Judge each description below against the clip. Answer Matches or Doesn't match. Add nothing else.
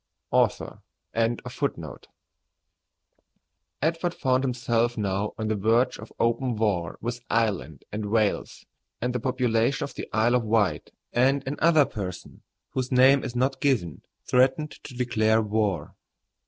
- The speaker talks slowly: Matches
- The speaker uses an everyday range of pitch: Matches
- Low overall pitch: Matches